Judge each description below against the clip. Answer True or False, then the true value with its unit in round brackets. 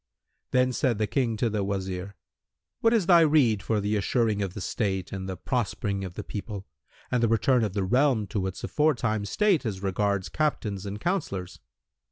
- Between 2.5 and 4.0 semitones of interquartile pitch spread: False (4.5 semitones)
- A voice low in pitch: True (105 Hz)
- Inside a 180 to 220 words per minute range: True (190 wpm)